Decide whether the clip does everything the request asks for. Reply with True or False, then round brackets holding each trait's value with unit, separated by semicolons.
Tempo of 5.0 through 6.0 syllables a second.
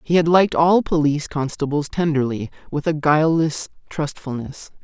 True (5.2 syllables/s)